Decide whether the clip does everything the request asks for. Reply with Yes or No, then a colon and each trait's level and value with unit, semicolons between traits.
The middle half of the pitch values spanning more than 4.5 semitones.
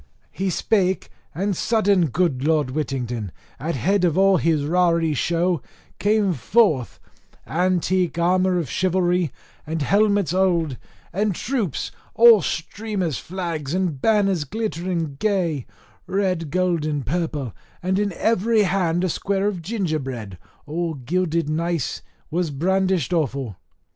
No: average, 3.8 semitones